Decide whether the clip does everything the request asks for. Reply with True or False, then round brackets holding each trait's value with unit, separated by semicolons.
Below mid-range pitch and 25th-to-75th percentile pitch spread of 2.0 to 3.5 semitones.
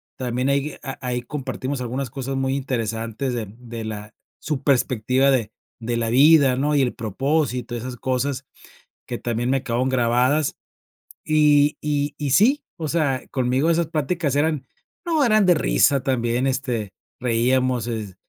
True (130 Hz; 3.1 semitones)